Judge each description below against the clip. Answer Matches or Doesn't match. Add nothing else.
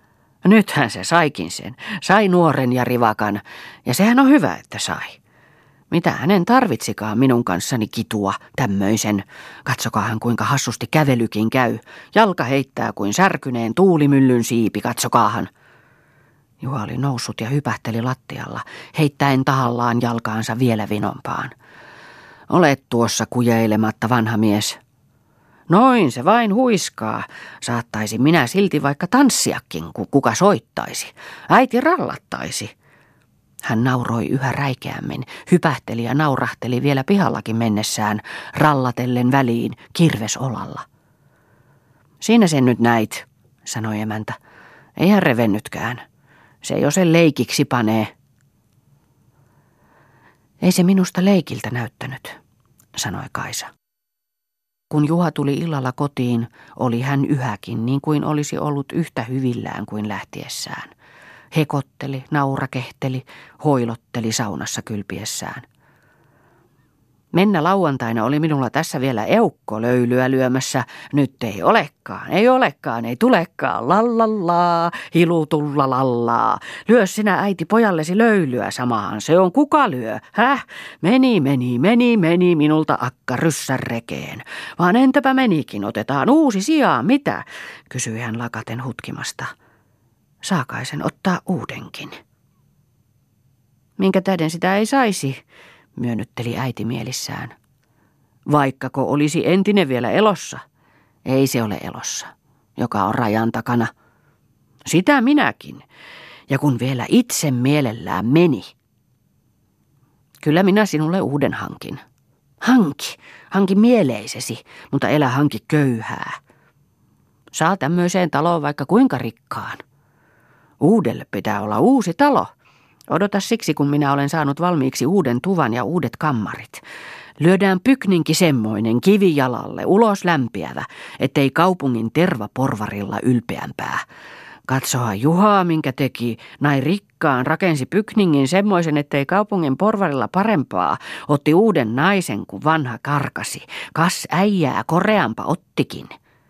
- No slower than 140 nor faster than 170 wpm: Doesn't match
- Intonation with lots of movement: Matches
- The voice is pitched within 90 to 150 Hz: Matches